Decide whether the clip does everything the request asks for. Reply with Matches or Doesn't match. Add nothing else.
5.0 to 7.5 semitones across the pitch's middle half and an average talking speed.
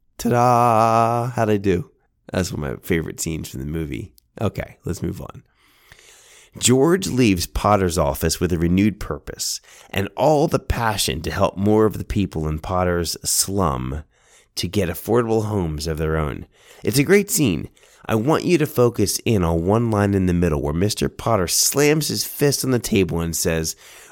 Matches